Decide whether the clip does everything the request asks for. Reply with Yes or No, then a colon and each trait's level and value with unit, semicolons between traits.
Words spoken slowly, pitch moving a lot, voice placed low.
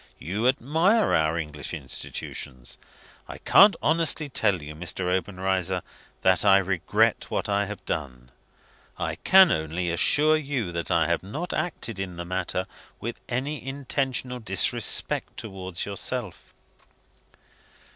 Yes: slow, 125 wpm; wide, 7.4 semitones; very low, 95 Hz